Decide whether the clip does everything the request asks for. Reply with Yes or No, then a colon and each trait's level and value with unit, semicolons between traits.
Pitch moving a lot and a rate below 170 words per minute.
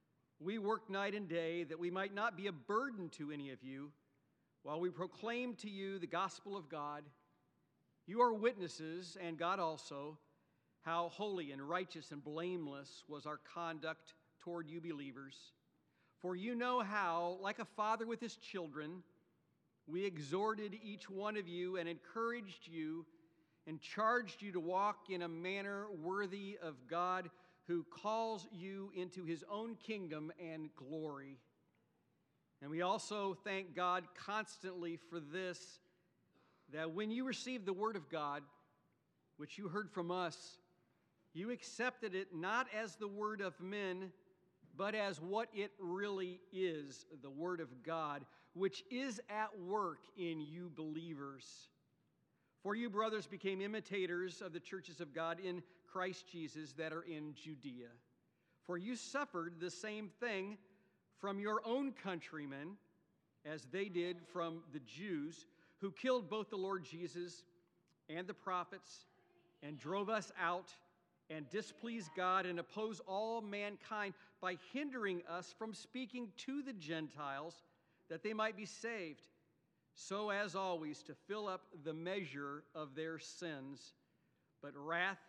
No: average, 3.9 semitones; average, 145 wpm